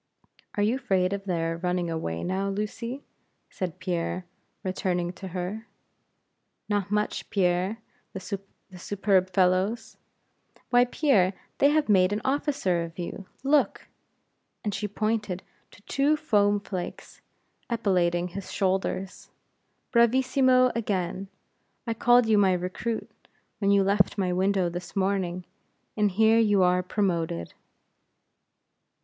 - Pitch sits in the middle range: No, high, 195 Hz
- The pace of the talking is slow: Yes, slow, 120 wpm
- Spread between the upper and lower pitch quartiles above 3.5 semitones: No, average, 3.2 semitones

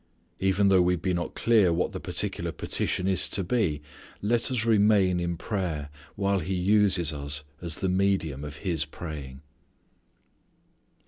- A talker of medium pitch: No, very low, 90 Hz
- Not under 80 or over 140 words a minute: No, average, 150 wpm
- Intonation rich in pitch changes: No, average, 3.8 semitones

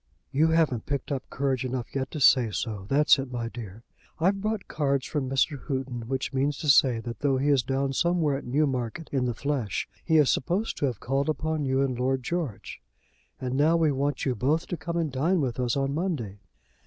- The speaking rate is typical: No, fast, 220 wpm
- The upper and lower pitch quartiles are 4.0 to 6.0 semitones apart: No, average, 3.3 semitones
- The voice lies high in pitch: No, low, 135 Hz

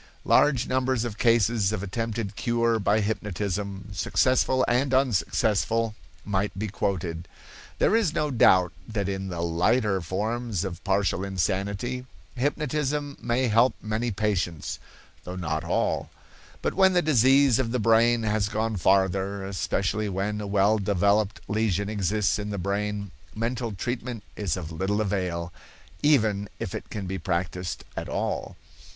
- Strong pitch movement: No, average, 3.5 semitones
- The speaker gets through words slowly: No, average, 145 wpm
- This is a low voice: Yes, low, 105 Hz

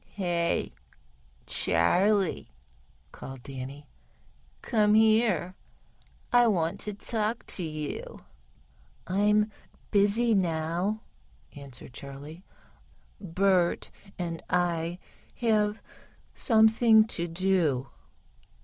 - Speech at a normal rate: No, slow, 75 wpm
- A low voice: No, medium, 185 Hz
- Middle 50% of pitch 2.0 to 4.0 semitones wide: No, average, 4.8 semitones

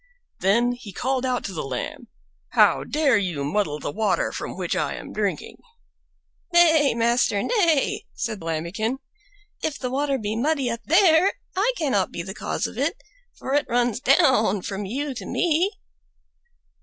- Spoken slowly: No, average, 160 wpm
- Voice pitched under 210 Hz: No, high, 245 Hz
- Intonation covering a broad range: Yes, wide, 6.4 semitones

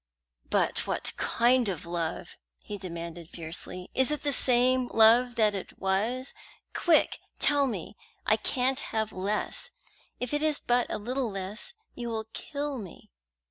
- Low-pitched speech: No, high, 225 Hz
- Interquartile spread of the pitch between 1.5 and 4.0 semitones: No, average, 5.0 semitones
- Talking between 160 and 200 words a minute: No, average, 150 wpm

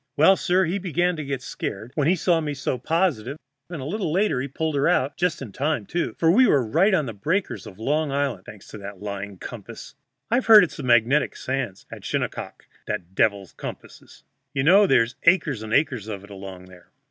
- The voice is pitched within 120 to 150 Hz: Yes, medium, 140 Hz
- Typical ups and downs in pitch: No, wide, 7.6 semitones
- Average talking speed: No, fast, 215 wpm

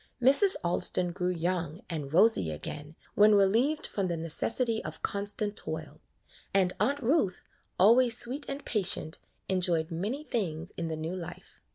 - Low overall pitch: No, medium, 185 Hz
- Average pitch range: No, wide, 5.8 semitones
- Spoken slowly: No, average, 155 wpm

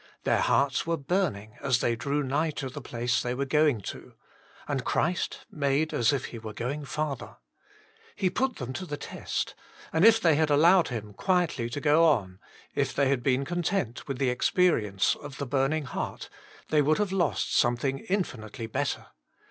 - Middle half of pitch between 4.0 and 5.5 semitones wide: Yes, average, 4.5 semitones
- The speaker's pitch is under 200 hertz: Yes, medium, 140 Hz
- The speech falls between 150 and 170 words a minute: No, average, 190 wpm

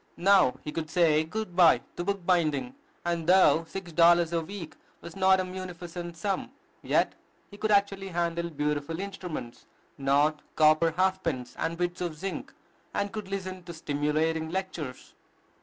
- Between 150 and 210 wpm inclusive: Yes, average, 155 wpm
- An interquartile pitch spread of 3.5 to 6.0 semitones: No, average, 3.1 semitones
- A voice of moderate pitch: Yes, medium, 170 Hz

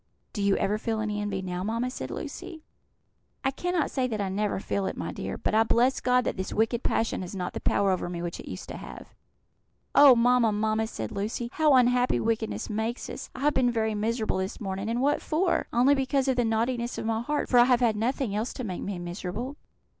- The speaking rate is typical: No, fast, 230 wpm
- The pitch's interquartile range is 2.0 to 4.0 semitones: Yes, average, 3.5 semitones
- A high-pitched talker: Yes, high, 225 Hz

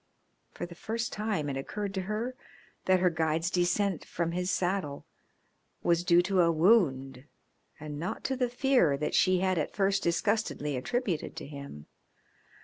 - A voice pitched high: No, medium, 180 Hz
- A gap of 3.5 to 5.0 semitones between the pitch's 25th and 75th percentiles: Yes, average, 4.7 semitones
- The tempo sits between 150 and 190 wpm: Yes, average, 160 wpm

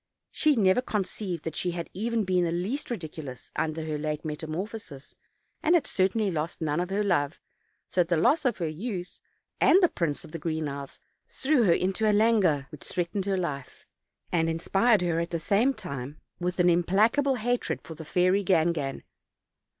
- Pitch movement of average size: Yes, average, 4.9 semitones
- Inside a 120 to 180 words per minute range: No, average, 190 wpm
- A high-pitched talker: No, medium, 180 Hz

